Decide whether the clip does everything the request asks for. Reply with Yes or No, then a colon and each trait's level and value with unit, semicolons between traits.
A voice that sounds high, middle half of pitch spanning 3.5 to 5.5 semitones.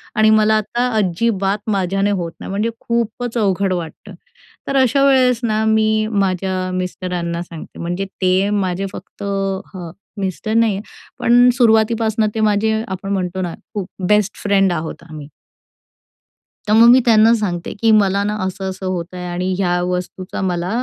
No: high, 195 Hz; average, 2.9 semitones